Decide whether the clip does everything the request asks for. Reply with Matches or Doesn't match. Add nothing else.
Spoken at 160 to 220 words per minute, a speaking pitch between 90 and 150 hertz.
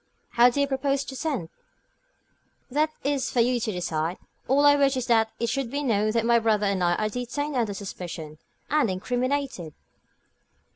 Doesn't match